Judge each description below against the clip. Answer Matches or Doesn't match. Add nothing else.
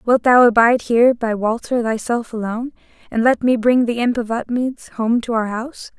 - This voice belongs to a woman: Matches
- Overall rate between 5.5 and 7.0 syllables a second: Doesn't match